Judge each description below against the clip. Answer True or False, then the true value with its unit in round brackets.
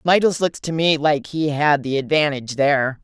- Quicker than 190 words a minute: True (200 wpm)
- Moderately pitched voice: True (150 Hz)